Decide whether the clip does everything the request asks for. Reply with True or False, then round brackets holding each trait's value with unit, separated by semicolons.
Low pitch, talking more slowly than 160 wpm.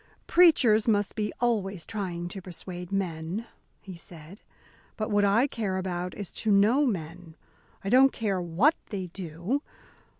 False (195 Hz; 145 wpm)